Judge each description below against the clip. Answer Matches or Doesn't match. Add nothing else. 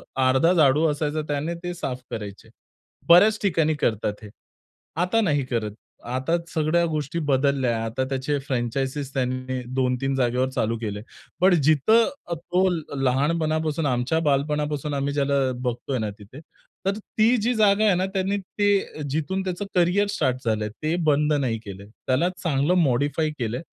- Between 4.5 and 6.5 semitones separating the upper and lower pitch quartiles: Matches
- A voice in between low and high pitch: Matches